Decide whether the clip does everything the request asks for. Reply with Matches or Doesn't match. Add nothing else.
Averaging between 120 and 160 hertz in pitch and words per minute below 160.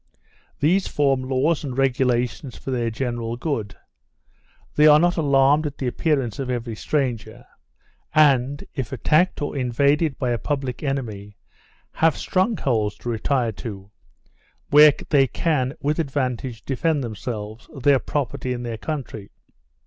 Matches